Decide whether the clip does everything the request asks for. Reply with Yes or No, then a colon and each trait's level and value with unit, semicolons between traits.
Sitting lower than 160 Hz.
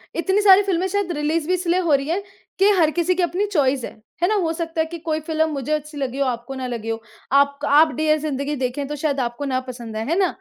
No: very high, 305 Hz